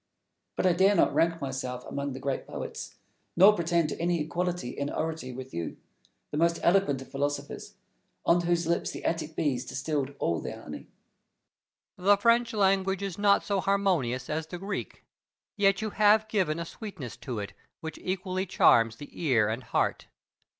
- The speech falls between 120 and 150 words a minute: No, average, 175 wpm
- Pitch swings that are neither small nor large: No, wide, 5.9 semitones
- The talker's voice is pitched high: No, medium, 170 Hz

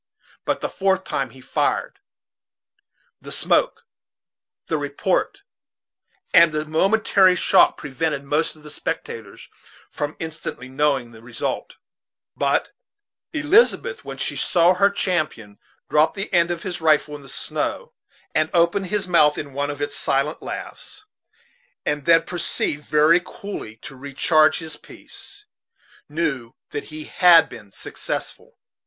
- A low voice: No, medium, 155 Hz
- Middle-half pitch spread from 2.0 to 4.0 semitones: Yes, average, 3.7 semitones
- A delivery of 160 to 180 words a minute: No, slow, 135 wpm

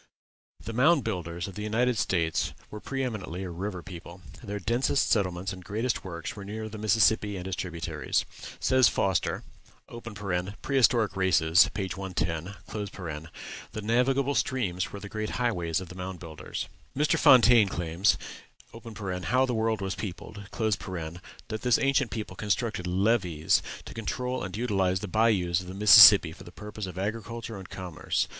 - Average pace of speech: Yes, average, 155 wpm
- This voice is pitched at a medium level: No, low, 100 Hz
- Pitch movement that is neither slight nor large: Yes, average, 3.9 semitones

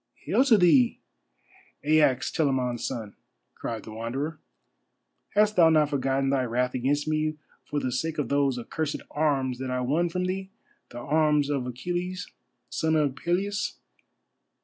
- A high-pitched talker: No, medium, 145 Hz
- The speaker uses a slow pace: No, average, 150 wpm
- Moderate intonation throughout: Yes, average, 4.2 semitones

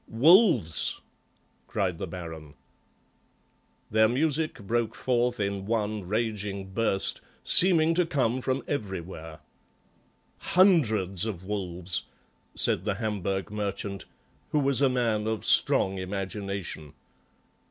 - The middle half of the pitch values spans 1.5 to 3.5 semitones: No, average, 4.4 semitones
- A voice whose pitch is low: Yes, low, 105 Hz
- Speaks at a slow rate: Yes, slow, 105 wpm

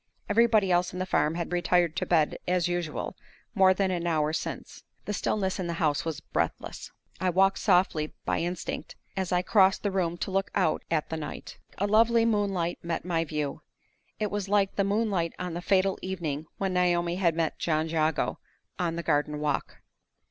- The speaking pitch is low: No, medium, 180 Hz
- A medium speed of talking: Yes, average, 190 wpm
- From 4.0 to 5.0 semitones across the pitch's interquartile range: No, average, 2.8 semitones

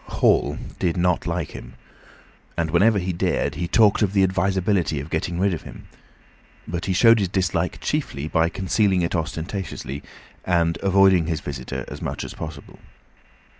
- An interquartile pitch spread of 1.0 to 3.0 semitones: Yes, average, 2.7 semitones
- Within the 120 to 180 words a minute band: Yes, average, 165 wpm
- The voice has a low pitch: Yes, very low, 90 Hz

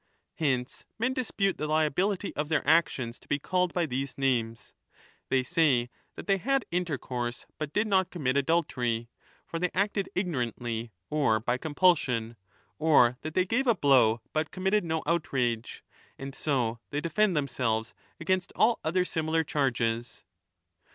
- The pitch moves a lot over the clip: Yes, wide, 6.5 semitones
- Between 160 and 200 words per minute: No, average, 150 wpm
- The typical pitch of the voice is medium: Yes, medium, 150 Hz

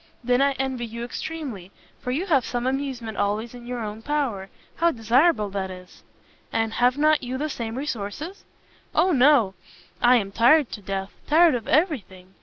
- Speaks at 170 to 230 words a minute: Yes, average, 180 wpm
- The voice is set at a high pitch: Yes, high, 245 Hz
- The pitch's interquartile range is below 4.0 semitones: No, average, 5.1 semitones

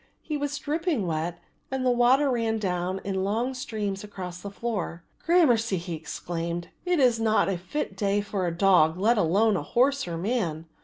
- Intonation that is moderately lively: No, wide, 5.7 semitones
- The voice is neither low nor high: No, high, 205 Hz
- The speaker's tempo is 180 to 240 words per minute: Yes, average, 190 wpm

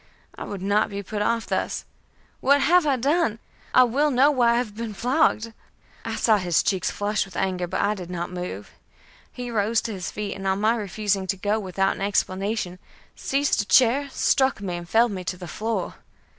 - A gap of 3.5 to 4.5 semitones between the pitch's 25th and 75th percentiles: Yes, average, 3.8 semitones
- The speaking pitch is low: No, high, 210 Hz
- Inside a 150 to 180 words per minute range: No, fast, 205 wpm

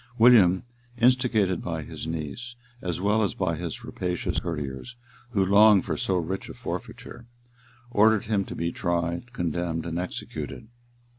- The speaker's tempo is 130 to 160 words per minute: Yes, average, 145 wpm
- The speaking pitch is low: Yes, very low, 90 Hz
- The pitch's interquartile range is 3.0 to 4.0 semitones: No, average, 4.4 semitones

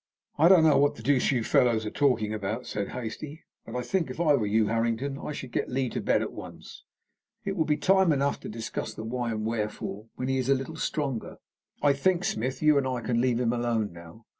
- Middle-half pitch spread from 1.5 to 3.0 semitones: No, average, 4.3 semitones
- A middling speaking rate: No, fast, 240 wpm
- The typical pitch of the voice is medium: No, low, 125 Hz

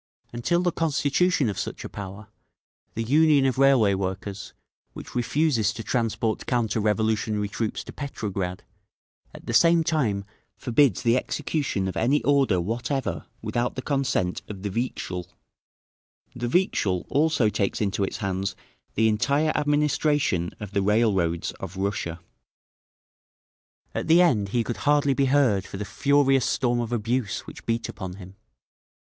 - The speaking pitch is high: No, low, 115 Hz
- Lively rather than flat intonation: Yes, wide, 5.9 semitones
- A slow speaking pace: No, average, 145 wpm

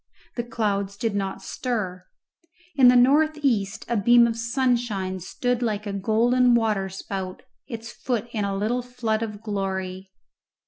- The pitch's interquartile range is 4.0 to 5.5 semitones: No, average, 3.5 semitones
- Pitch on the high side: Yes, high, 220 Hz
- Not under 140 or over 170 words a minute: Yes, average, 145 wpm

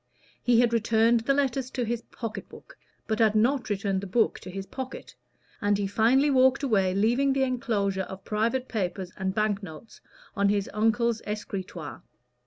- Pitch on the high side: Yes, high, 220 Hz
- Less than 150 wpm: No, average, 175 wpm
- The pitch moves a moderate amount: Yes, average, 3.6 semitones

